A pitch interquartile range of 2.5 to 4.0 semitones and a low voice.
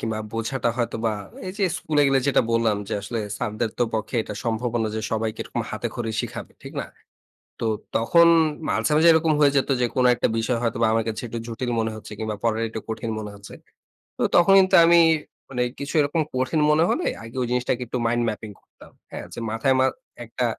Yes: average, 3.2 semitones; low, 120 Hz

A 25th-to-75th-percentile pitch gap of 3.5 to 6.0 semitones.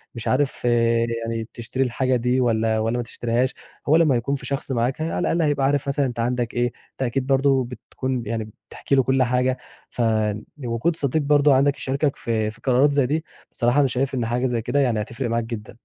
No: average, 2.9 semitones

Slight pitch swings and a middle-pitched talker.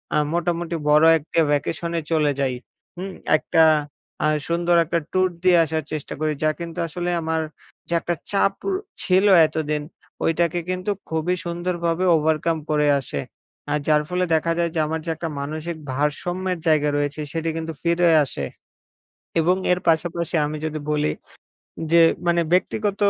Yes: narrow, 2.1 semitones; medium, 165 Hz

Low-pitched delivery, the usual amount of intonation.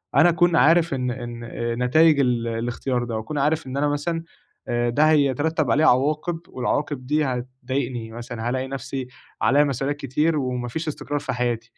Yes: low, 130 Hz; average, 3.6 semitones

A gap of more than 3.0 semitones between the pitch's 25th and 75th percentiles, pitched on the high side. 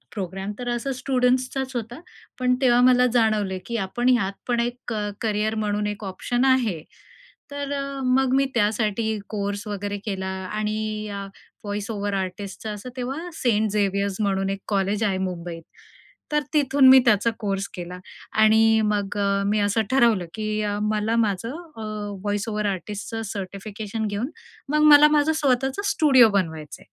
Yes: average, 3.7 semitones; high, 215 Hz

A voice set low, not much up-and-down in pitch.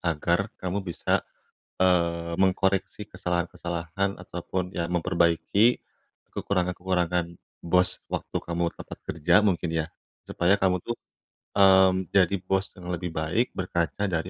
Yes: very low, 90 Hz; narrow, 1.9 semitones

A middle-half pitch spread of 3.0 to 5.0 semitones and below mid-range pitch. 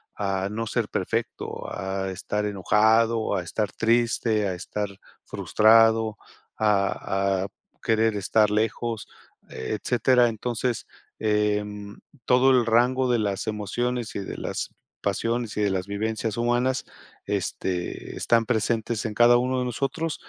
No: narrow, 2.5 semitones; low, 110 Hz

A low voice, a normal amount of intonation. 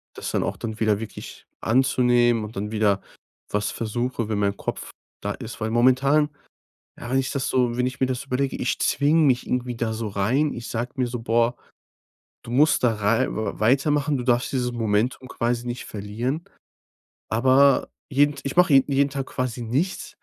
Yes: low, 125 Hz; average, 3.0 semitones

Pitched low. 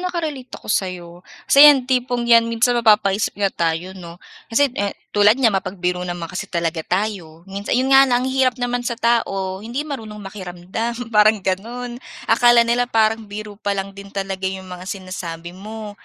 No: high, 210 Hz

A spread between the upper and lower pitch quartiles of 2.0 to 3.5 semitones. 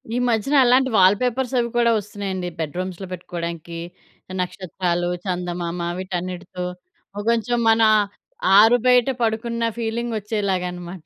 No: average, 4.6 semitones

